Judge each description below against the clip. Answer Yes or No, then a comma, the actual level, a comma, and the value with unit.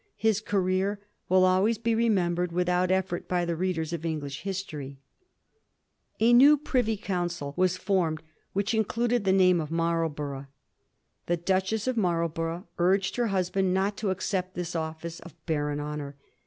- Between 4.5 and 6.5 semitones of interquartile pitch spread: No, average, 3.0 semitones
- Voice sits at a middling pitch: Yes, medium, 180 Hz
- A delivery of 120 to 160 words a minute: Yes, average, 155 wpm